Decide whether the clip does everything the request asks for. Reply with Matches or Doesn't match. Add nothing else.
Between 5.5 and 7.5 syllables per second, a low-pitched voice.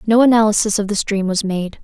Doesn't match